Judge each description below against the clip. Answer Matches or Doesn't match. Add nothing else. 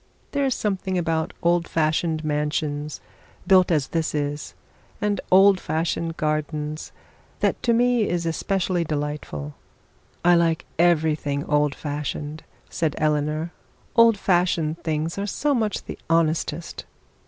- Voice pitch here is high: Doesn't match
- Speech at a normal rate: Doesn't match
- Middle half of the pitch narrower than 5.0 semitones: Matches